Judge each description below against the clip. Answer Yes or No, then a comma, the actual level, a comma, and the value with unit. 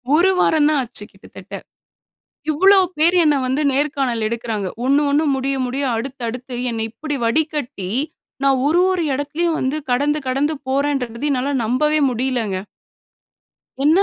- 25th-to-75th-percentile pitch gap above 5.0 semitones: No, average, 3.5 semitones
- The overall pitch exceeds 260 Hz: Yes, very high, 275 Hz